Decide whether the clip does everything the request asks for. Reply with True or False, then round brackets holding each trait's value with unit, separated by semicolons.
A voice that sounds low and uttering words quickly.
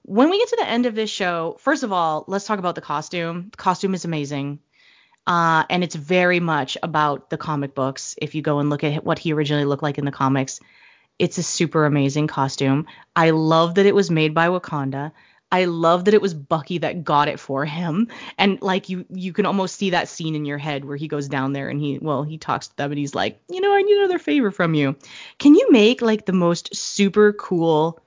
False (165 Hz; 235 wpm)